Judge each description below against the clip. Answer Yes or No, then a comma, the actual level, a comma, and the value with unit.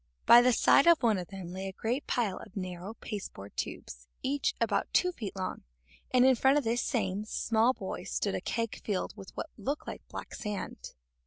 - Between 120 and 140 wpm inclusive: No, average, 200 wpm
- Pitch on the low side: No, high, 220 Hz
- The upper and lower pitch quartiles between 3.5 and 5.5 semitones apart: Yes, average, 4.7 semitones